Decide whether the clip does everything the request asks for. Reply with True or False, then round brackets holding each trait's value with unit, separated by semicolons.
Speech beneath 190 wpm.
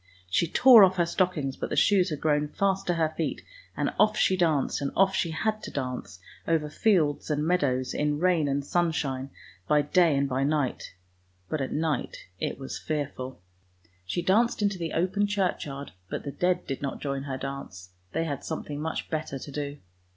False (195 wpm)